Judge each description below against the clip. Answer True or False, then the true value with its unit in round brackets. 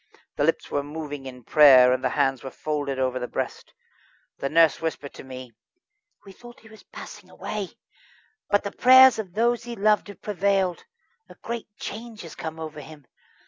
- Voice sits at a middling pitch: True (160 Hz)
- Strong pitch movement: True (7.4 semitones)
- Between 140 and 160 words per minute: False (185 wpm)